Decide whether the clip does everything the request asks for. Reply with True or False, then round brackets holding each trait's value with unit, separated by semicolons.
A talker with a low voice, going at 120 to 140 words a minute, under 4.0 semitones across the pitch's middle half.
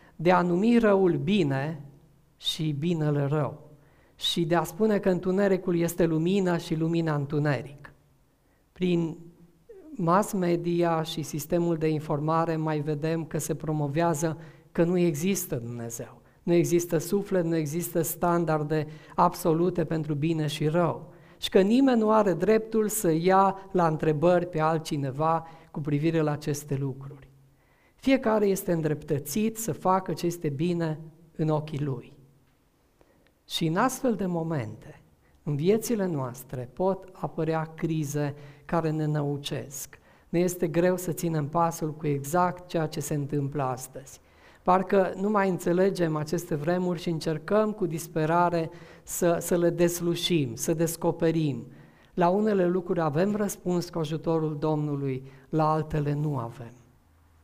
False (165 Hz; 135 wpm; 2.7 semitones)